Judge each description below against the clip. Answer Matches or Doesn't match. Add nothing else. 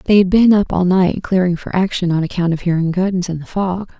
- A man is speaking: Doesn't match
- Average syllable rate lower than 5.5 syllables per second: Doesn't match